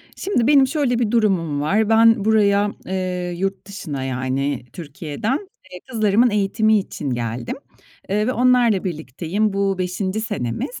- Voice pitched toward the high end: Yes, high, 200 Hz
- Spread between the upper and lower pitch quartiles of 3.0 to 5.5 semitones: Yes, average, 5.1 semitones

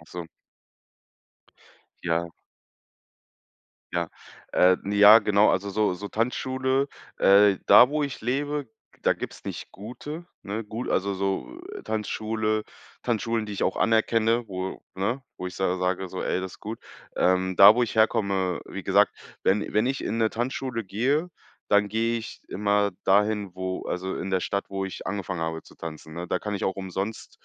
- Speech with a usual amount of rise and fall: Yes, average, 3.3 semitones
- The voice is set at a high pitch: No, low, 105 Hz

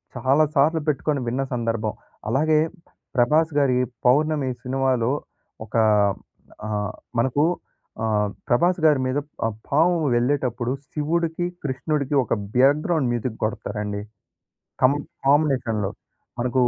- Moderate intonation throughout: Yes, average, 4.1 semitones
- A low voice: Yes, low, 130 Hz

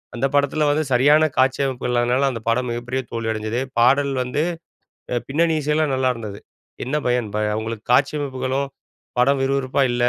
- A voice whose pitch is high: No, low, 130 Hz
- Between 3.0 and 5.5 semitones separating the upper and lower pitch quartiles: No, narrow, 2.4 semitones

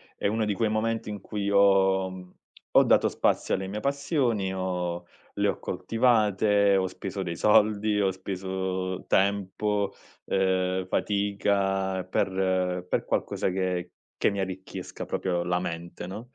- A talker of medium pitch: No, very low, 95 Hz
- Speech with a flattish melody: Yes, narrow, 1.8 semitones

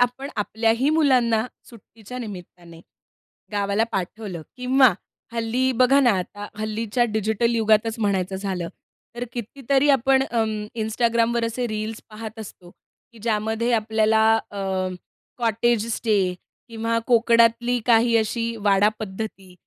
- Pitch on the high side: Yes, high, 225 Hz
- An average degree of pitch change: No, narrow, 2.2 semitones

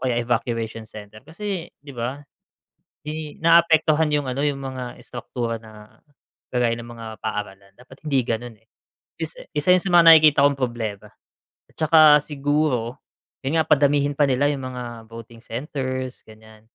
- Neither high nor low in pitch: No, low, 130 Hz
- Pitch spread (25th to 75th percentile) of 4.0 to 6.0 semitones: Yes, average, 4.3 semitones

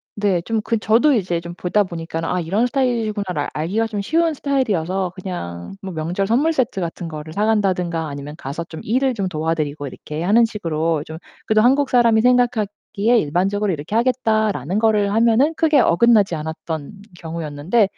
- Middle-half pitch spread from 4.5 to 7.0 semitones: Yes, wide, 5.6 semitones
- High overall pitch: Yes, high, 195 Hz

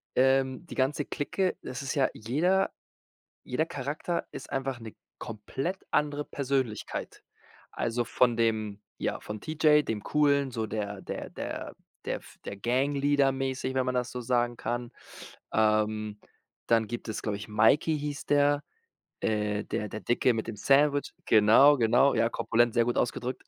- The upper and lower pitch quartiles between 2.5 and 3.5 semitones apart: No, average, 4.2 semitones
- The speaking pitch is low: Yes, low, 125 Hz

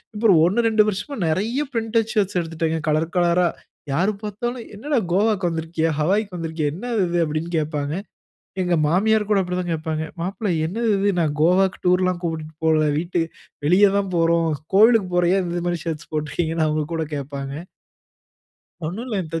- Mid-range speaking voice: Yes, medium, 175 Hz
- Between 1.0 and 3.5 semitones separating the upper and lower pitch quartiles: No, average, 4.2 semitones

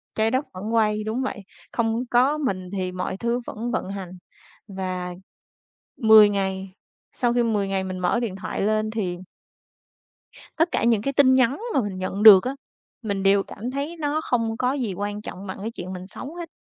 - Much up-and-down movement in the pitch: No, average, 4.2 semitones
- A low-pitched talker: No, high, 215 Hz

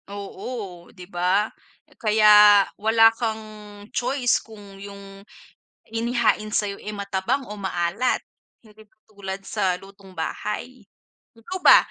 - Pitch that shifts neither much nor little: No, narrow, 2.3 semitones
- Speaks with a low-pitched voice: No, high, 210 Hz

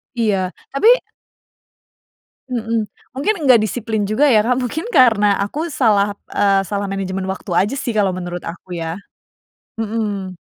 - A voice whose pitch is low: No, high, 210 Hz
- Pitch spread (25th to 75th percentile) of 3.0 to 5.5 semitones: Yes, average, 3.5 semitones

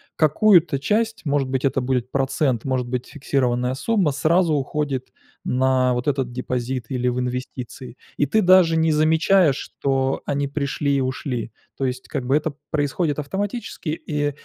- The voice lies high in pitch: No, medium, 140 Hz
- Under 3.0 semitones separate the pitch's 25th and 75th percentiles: No, average, 3.4 semitones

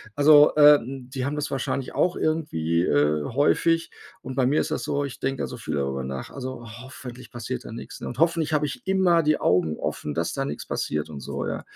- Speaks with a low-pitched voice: Yes, low, 130 Hz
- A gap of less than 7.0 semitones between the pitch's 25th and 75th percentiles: No, wide, 8.6 semitones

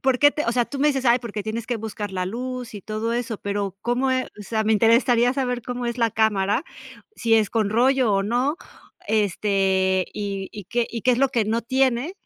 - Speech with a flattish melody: No, average, 3.2 semitones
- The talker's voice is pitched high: Yes, high, 230 Hz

